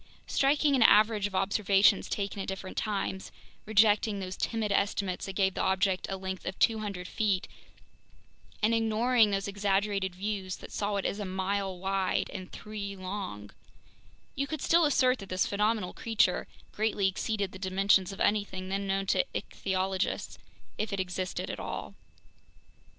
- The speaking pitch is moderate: No, high, 200 Hz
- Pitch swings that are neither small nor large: No, narrow, 2.1 semitones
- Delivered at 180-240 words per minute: No, average, 150 wpm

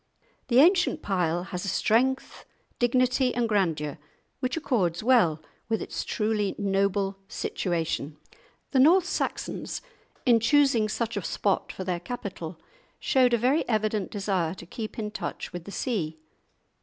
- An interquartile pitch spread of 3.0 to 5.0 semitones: No, wide, 5.6 semitones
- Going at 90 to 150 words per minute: Yes, average, 145 wpm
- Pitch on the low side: No, high, 210 Hz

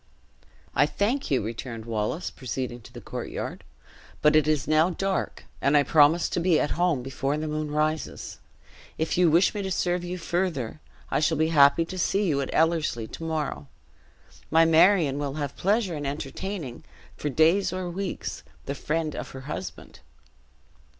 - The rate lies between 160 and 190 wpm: Yes, average, 170 wpm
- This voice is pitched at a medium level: Yes, medium, 155 Hz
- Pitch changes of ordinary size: Yes, average, 3.9 semitones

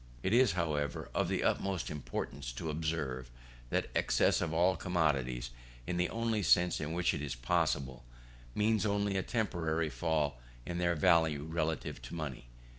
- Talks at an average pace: Yes, average, 160 wpm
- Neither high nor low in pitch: No, very low, 80 Hz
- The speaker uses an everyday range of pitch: Yes, average, 3.8 semitones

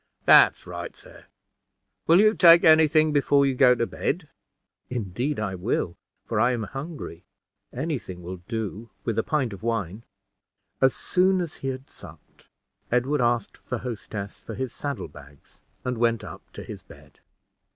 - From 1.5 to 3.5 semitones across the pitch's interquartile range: No, average, 5.2 semitones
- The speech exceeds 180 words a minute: No, average, 165 wpm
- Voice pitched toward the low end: Yes, low, 125 Hz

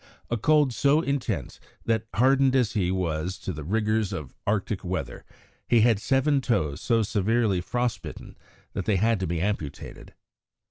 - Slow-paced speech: No, average, 160 wpm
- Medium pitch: No, low, 110 Hz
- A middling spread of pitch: Yes, average, 4.8 semitones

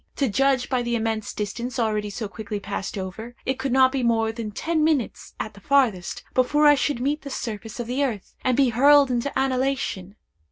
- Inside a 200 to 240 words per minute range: Yes, fast, 205 wpm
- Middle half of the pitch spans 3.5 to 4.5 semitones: Yes, average, 3.8 semitones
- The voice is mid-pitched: No, high, 245 Hz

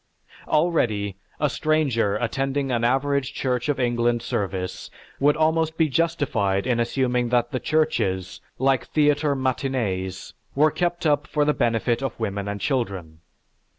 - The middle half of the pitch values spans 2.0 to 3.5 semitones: No, average, 4.6 semitones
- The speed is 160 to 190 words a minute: No, average, 140 wpm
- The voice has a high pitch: No, low, 130 Hz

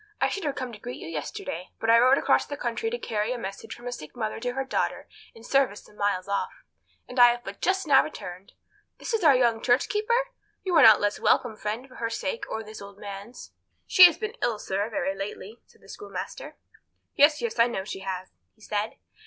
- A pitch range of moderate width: Yes, average, 4.9 semitones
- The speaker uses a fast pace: Yes, fast, 235 wpm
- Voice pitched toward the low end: No, high, 230 Hz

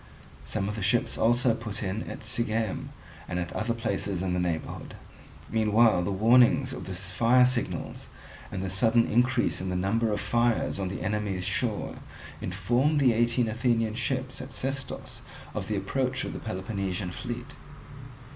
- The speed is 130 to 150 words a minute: No, average, 165 wpm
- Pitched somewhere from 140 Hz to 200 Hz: No, low, 110 Hz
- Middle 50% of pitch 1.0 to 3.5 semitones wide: No, average, 4.0 semitones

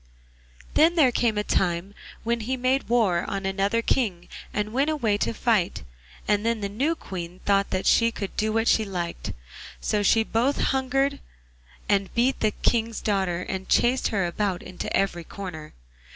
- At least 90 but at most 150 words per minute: No, average, 170 wpm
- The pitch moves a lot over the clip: No, average, 3.8 semitones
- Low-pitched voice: No, high, 210 Hz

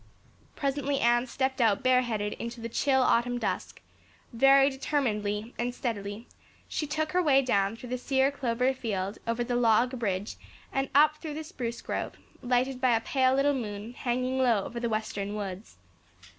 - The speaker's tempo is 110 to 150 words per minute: No, average, 170 wpm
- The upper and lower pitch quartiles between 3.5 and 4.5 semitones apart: No, average, 3.0 semitones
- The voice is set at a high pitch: Yes, high, 245 Hz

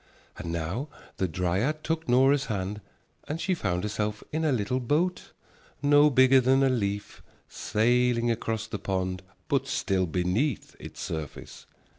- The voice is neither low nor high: No, low, 115 Hz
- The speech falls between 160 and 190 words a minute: No, average, 145 wpm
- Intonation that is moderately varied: No, wide, 6.1 semitones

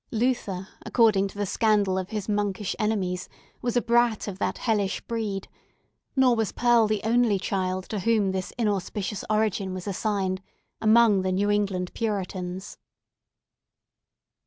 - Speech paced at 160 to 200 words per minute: No, average, 140 wpm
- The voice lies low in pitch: No, high, 205 Hz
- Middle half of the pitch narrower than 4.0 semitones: Yes, average, 2.8 semitones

